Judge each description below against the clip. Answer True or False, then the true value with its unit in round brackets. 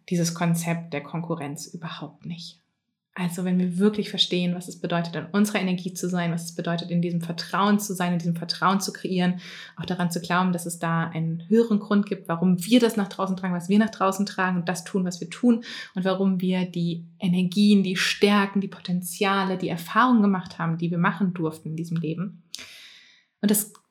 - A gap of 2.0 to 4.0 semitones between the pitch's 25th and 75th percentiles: True (2.5 semitones)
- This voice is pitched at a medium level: True (180 Hz)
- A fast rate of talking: True (205 wpm)